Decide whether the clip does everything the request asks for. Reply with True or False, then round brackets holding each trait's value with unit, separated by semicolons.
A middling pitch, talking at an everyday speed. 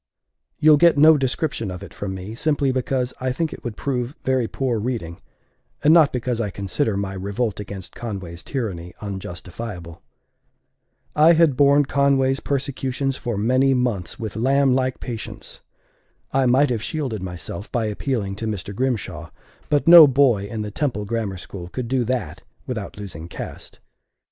False (120 Hz; 160 wpm)